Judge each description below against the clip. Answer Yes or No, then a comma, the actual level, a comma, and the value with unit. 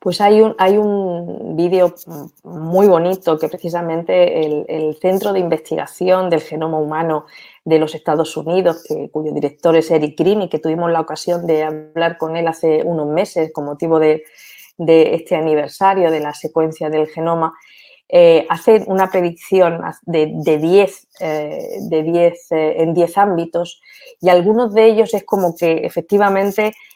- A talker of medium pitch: Yes, medium, 170 Hz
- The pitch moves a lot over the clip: No, average, 2.9 semitones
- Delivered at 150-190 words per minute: Yes, average, 165 wpm